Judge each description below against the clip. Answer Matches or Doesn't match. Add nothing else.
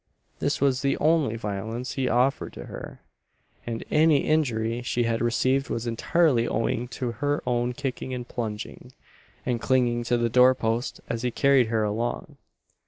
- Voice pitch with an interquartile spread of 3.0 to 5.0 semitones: Doesn't match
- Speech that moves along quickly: Doesn't match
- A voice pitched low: Matches